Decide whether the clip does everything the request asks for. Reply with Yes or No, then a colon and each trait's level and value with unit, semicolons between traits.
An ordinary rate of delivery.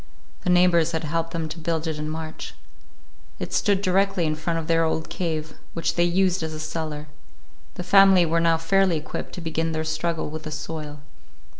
Yes: average, 195 wpm